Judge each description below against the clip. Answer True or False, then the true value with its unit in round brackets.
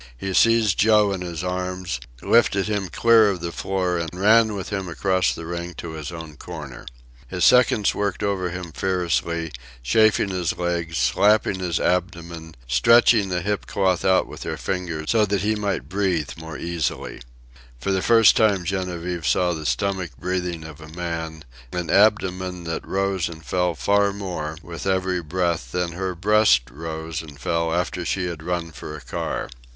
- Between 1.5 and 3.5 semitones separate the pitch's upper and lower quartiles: True (2.8 semitones)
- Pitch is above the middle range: False (90 Hz)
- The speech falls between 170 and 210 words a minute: True (175 wpm)